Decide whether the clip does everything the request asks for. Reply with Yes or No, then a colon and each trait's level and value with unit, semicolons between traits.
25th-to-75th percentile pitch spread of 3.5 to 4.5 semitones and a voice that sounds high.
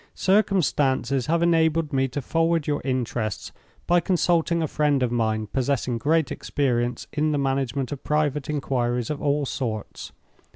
No: average, 4.1 semitones; medium, 140 Hz